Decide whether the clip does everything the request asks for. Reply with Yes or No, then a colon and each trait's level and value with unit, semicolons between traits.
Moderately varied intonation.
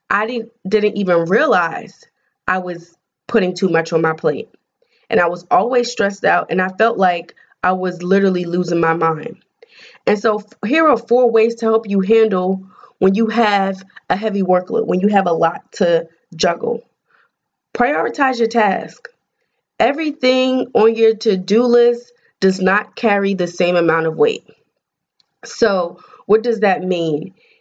Yes: average, 4.2 semitones